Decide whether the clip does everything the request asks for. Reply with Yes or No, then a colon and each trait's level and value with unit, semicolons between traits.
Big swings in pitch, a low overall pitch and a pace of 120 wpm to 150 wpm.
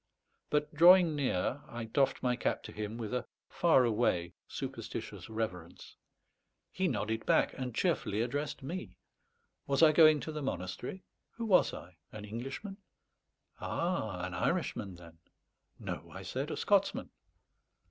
Yes: wide, 6.6 semitones; low, 125 Hz; average, 140 wpm